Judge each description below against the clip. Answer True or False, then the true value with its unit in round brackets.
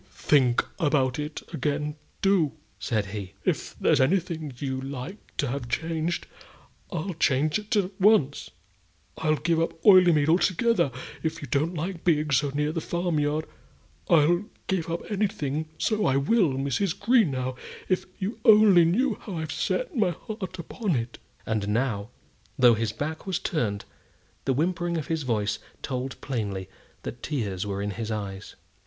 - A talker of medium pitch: True (155 Hz)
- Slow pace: False (160 wpm)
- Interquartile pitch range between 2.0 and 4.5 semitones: False (5.6 semitones)